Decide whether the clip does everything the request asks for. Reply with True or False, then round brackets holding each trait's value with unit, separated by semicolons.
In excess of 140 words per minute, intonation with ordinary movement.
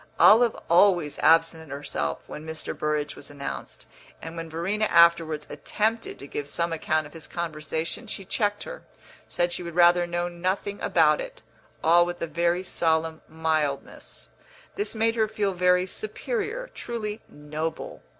True (150 wpm; 4.3 semitones)